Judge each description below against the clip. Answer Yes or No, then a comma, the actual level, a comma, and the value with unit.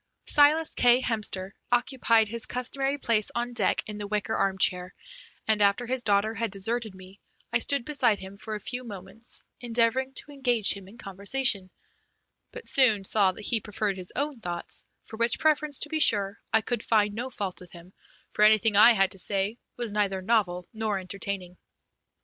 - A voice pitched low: No, high, 215 Hz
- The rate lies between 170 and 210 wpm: Yes, average, 180 wpm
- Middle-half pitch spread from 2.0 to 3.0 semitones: No, average, 3.6 semitones